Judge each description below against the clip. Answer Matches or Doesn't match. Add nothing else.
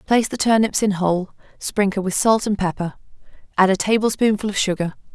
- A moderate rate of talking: Matches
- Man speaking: Doesn't match